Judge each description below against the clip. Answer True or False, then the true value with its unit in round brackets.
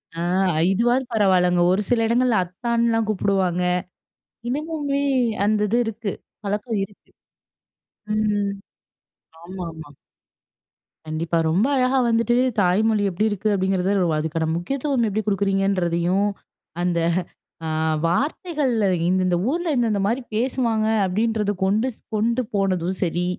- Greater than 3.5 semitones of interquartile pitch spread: True (4.2 semitones)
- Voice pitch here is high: True (205 Hz)